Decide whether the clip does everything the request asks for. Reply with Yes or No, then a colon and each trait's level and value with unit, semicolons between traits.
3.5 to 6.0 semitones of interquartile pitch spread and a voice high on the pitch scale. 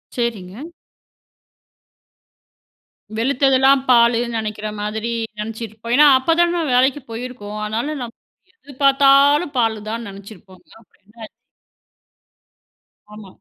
Yes: average, 4.2 semitones; high, 235 Hz